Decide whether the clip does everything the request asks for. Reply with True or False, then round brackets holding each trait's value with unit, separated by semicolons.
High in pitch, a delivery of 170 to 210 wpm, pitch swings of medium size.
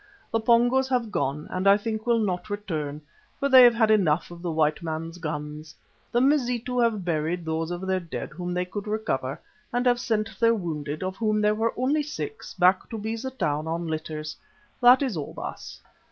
False (200 Hz; 195 wpm; 6.3 semitones)